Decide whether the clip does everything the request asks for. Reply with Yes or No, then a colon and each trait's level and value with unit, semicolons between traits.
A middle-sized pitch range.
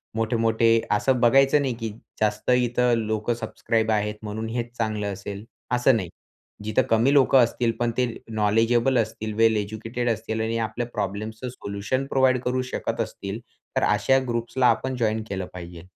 No: narrow, 2.3 semitones